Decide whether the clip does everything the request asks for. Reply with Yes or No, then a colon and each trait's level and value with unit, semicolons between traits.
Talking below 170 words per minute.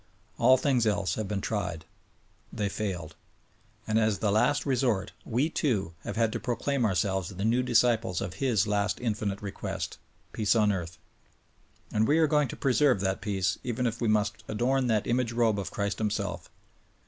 No: average, 175 wpm